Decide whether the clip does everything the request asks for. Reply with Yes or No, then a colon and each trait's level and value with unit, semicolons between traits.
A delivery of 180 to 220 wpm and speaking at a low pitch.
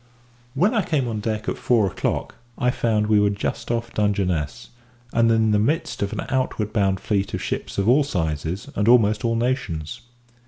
Yes: average, 190 wpm; low, 110 Hz